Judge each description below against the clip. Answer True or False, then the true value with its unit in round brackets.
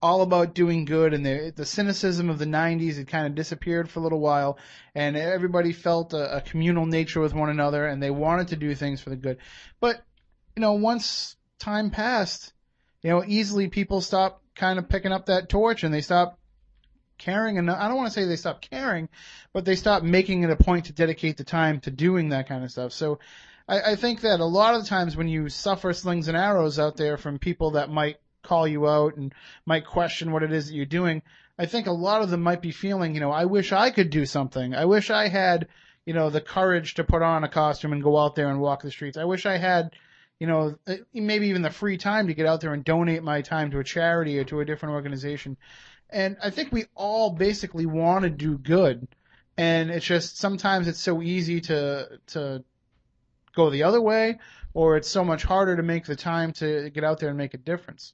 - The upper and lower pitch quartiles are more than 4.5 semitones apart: False (3.8 semitones)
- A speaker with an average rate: False (230 wpm)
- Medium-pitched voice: True (165 Hz)